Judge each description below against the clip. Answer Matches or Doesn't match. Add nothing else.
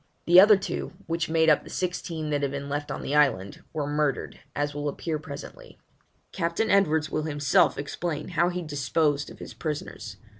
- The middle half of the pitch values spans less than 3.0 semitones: Matches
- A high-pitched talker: Doesn't match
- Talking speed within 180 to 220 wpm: Matches